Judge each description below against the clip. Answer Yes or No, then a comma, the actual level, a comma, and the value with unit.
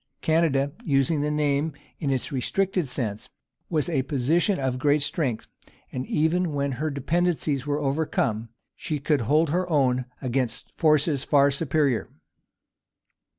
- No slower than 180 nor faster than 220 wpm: No, slow, 135 wpm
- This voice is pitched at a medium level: Yes, medium, 145 Hz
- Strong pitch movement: No, average, 3.0 semitones